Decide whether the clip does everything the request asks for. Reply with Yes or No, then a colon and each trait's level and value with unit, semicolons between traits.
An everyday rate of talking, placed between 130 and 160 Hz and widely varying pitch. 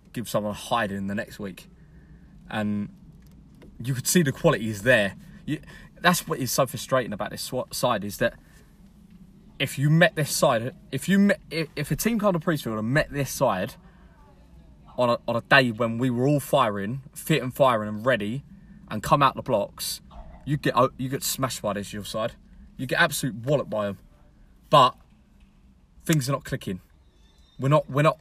Yes: average, 190 wpm; low, 135 Hz; wide, 6.7 semitones